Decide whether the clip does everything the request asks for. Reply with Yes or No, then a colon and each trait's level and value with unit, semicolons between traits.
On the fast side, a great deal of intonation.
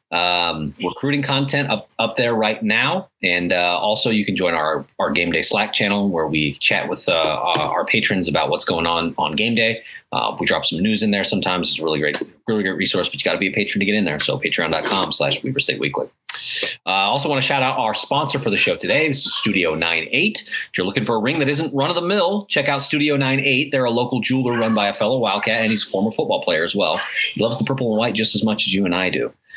Yes: fast, 260 wpm; wide, 5.9 semitones